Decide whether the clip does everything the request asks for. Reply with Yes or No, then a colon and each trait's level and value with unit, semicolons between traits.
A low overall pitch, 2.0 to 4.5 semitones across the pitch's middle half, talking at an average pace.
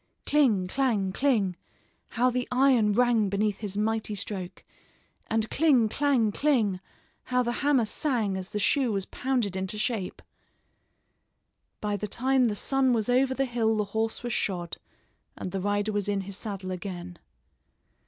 No: high, 215 Hz; average, 3.9 semitones; average, 155 wpm